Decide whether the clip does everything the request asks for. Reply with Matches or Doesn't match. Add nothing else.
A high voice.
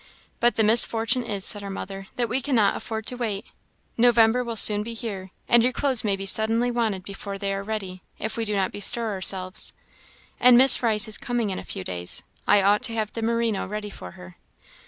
Matches